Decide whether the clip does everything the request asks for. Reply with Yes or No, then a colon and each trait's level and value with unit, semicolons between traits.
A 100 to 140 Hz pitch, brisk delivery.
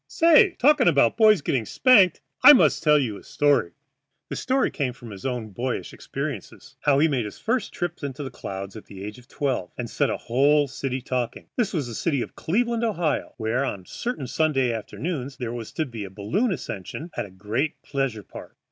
Yes: low, 135 Hz; fast, 210 wpm